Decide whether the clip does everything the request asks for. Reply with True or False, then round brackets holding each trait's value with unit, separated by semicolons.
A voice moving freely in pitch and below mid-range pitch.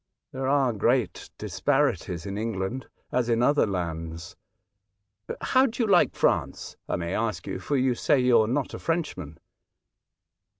True (5.9 semitones; 115 Hz)